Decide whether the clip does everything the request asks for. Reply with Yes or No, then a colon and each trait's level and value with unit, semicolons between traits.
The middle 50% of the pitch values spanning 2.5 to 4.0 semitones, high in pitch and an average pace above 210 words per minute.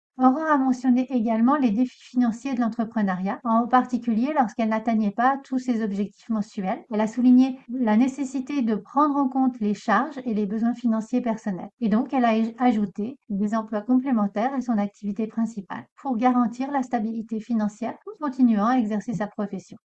No: average, 2.9 semitones; high, 235 Hz; average, 175 wpm